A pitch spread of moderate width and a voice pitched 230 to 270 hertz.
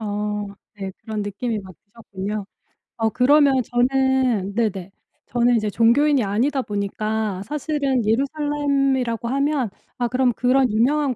Yes: average, 4.4 semitones; high, 235 Hz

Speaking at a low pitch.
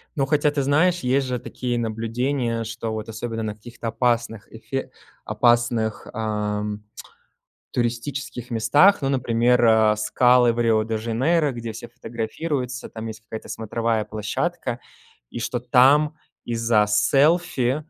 Yes: low, 120 Hz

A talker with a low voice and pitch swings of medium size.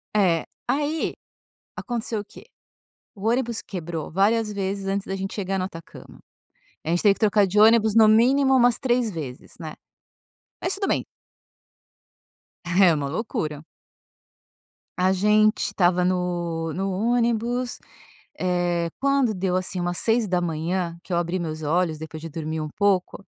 No: high, 190 Hz; average, 4.4 semitones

